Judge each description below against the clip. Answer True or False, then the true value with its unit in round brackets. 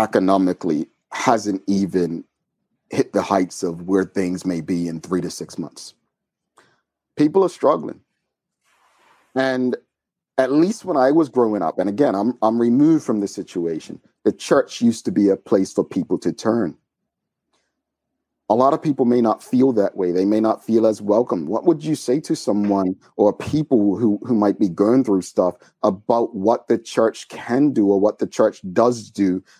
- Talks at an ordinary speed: True (180 wpm)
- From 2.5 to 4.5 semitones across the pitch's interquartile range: False (5.2 semitones)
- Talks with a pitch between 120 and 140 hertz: False (110 Hz)